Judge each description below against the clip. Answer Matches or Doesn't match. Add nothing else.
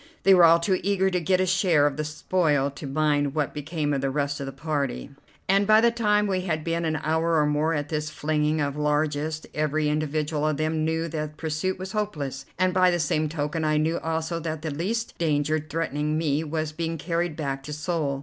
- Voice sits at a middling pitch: Matches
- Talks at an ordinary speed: Doesn't match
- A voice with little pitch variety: Matches